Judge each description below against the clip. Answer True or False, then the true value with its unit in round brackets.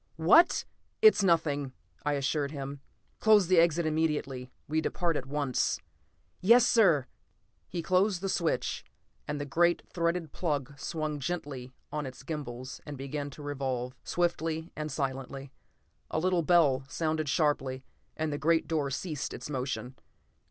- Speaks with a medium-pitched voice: True (150 Hz)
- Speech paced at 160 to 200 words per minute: False (145 wpm)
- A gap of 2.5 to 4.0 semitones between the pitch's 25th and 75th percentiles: True (3.6 semitones)